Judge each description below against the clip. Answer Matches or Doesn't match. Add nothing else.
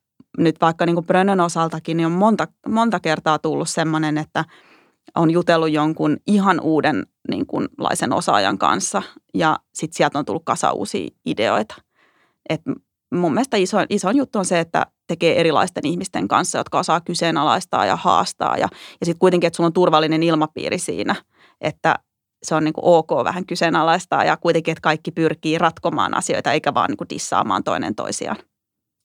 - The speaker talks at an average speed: Doesn't match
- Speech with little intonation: Matches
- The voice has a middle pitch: Matches